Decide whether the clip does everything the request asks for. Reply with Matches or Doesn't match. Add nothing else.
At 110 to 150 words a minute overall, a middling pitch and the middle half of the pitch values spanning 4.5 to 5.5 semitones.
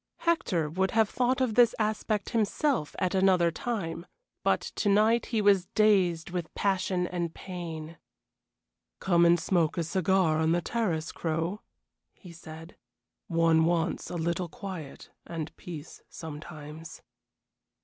Doesn't match